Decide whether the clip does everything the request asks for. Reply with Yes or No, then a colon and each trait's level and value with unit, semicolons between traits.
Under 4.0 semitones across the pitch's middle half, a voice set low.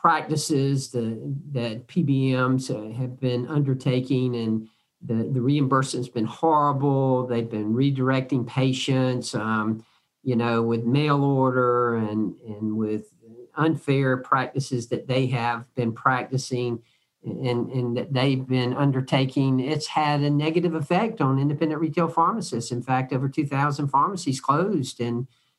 Yes: average, 2.7 semitones; low, 130 Hz